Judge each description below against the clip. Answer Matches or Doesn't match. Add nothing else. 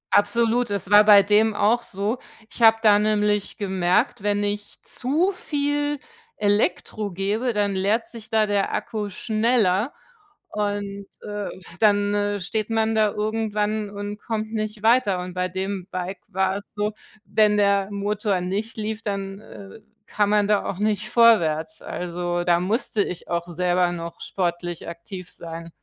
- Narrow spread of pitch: Matches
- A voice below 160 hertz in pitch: Doesn't match